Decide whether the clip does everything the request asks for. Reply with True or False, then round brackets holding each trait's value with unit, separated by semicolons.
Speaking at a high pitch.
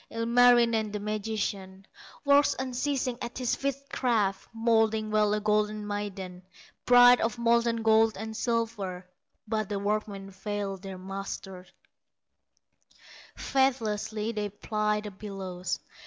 True (215 Hz)